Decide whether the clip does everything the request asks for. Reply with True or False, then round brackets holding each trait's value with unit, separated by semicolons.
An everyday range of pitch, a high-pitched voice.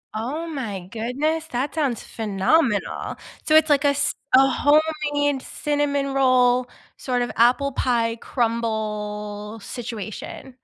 True (4.4 semitones; 250 Hz)